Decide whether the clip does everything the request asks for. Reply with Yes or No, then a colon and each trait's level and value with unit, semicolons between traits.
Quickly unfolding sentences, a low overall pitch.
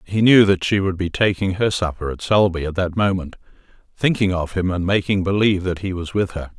Yes: fast, 230 wpm; very low, 95 Hz